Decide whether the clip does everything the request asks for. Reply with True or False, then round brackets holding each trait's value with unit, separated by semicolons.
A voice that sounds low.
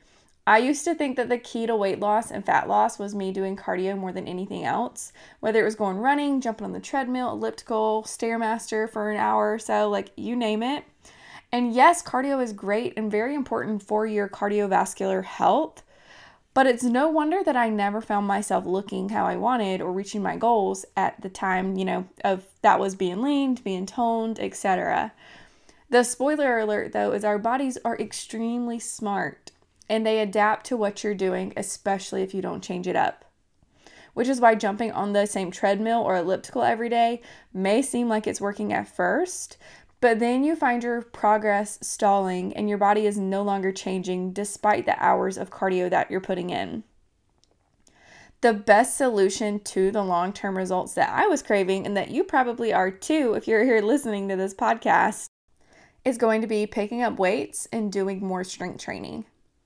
False (210 Hz)